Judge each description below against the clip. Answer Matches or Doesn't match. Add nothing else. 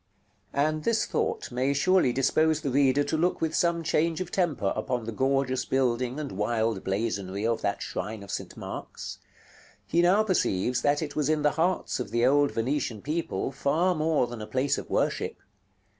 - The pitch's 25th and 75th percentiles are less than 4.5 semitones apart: Doesn't match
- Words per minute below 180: Doesn't match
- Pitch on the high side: Doesn't match